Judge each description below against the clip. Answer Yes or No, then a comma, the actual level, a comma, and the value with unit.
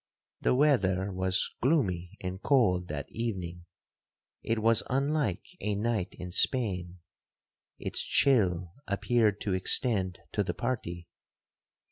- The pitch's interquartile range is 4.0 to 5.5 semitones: Yes, average, 4.6 semitones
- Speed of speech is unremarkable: No, slow, 110 wpm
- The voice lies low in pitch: Yes, low, 100 Hz